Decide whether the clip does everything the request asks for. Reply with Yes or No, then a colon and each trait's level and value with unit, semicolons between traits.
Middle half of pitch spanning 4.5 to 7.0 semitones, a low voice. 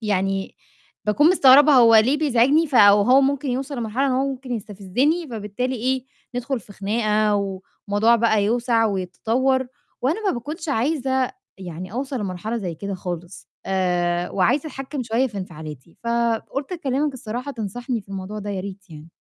No: average, 5.0 semitones; high, 230 Hz